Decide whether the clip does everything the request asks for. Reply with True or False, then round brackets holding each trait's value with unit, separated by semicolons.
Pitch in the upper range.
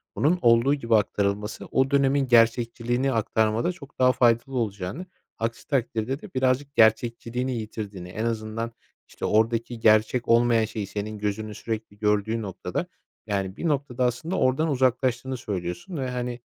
False (115 Hz)